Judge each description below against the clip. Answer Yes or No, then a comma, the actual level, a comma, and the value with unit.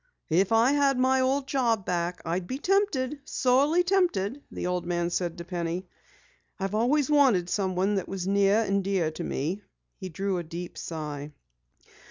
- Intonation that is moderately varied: No, wide, 6.8 semitones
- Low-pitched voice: No, high, 195 Hz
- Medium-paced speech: Yes, average, 170 wpm